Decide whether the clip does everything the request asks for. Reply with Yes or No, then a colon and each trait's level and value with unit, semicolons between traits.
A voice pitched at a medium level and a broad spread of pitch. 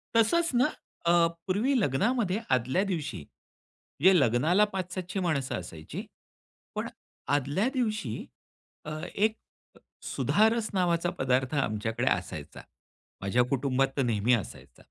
Yes: medium, 155 Hz; wide, 8.6 semitones